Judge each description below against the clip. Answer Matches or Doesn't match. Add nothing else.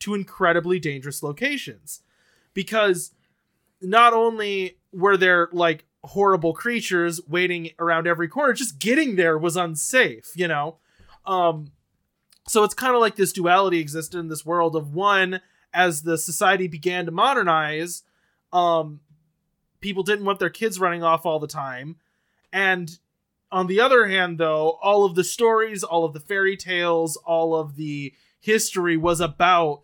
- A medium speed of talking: Matches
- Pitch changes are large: Doesn't match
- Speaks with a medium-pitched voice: Matches